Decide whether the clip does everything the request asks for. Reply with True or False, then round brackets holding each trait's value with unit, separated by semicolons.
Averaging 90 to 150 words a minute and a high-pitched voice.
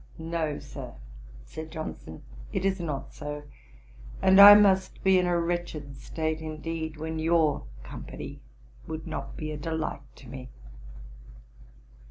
False (135 wpm; 160 Hz)